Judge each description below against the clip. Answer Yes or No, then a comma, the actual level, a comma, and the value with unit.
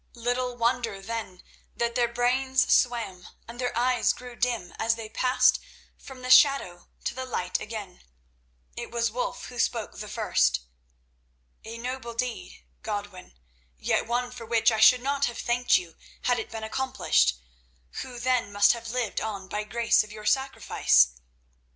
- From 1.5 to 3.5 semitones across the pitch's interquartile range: Yes, average, 2.7 semitones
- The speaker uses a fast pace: No, average, 160 wpm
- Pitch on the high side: Yes, high, 235 Hz